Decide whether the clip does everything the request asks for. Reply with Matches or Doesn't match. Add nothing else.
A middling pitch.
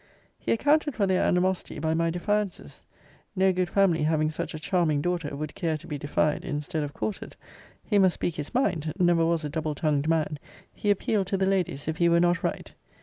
Matches